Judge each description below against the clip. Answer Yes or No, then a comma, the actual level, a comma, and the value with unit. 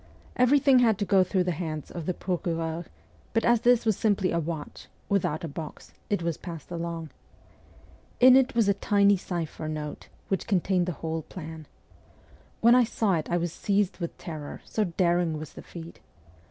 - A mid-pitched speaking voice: Yes, medium, 175 Hz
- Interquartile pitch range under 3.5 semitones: No, average, 3.9 semitones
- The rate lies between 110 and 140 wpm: No, average, 180 wpm